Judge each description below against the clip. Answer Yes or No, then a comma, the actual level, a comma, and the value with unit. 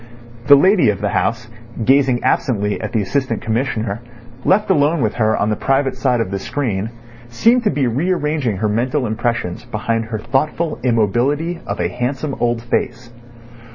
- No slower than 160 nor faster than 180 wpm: Yes, average, 165 wpm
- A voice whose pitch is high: No, low, 120 Hz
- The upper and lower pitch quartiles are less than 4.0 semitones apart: No, average, 4.3 semitones